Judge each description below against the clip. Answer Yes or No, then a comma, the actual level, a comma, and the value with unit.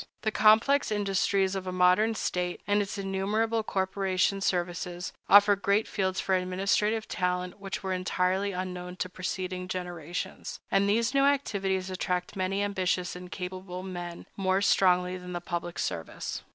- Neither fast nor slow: Yes, average, 150 wpm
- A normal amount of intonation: No, narrow, 1.8 semitones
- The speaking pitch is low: No, high, 190 Hz